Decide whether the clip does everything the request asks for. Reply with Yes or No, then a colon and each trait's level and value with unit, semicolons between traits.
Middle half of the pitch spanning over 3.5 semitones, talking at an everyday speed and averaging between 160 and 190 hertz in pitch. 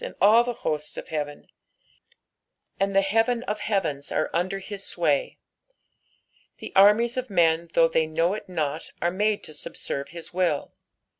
Yes: average, 4.7 semitones; average, 160 wpm; medium, 185 Hz